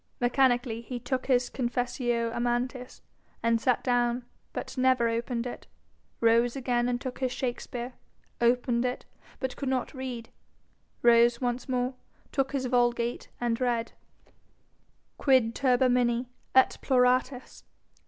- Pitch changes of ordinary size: No, narrow, 1.3 semitones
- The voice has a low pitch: No, high, 245 Hz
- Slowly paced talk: Yes, slow, 125 wpm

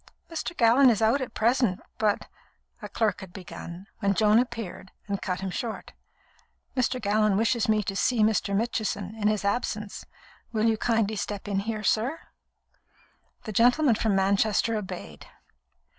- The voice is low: No, high, 215 Hz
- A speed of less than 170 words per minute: Yes, average, 160 wpm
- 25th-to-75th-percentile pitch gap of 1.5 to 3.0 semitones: Yes, narrow, 2.5 semitones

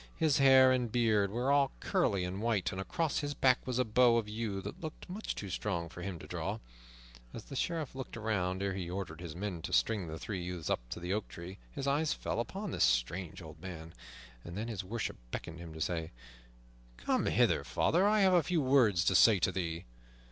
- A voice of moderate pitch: No, low, 105 Hz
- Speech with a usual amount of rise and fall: No, wide, 6.8 semitones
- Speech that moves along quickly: Yes, fast, 220 wpm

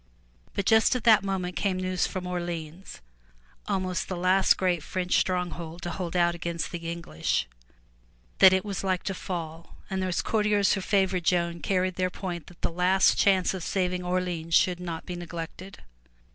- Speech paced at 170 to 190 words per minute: Yes, average, 175 wpm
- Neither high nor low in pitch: Yes, medium, 180 Hz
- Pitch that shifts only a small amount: Yes, narrow, 1.7 semitones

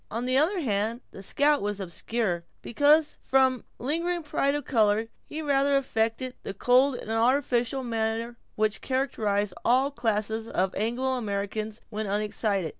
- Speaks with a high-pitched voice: Yes, high, 235 Hz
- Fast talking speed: No, average, 150 wpm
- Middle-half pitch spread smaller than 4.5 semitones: Yes, average, 4.1 semitones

